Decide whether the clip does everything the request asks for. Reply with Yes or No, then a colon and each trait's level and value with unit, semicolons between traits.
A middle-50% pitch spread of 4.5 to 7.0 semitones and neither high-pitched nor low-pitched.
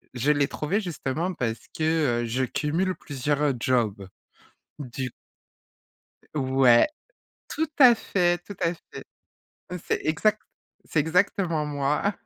Yes: average, 5.1 semitones; medium, 150 Hz